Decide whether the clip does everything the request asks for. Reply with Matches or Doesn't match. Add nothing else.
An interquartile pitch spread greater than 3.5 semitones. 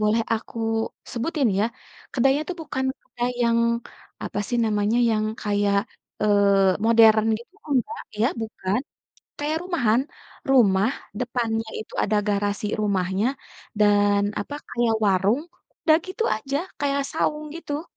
Matches